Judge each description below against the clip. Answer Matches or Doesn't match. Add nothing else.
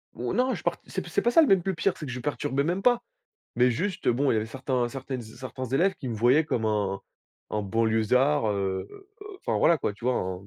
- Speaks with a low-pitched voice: Matches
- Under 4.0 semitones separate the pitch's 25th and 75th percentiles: Doesn't match